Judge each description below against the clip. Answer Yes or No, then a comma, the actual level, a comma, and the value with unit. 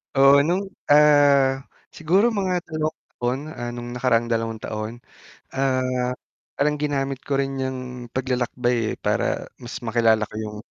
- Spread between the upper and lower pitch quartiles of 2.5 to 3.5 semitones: Yes, average, 2.9 semitones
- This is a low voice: Yes, low, 130 Hz